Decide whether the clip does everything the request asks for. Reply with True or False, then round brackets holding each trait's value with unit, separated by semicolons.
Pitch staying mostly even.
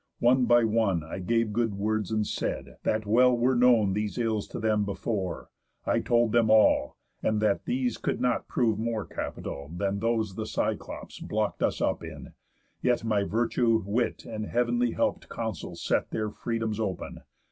True (2.2 semitones)